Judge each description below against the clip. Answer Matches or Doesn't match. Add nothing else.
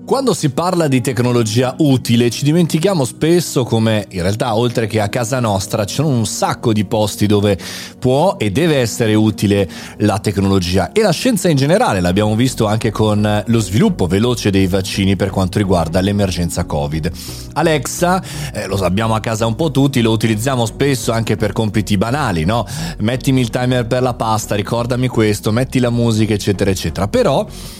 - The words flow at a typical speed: Doesn't match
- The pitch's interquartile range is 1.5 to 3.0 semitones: Doesn't match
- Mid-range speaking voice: Doesn't match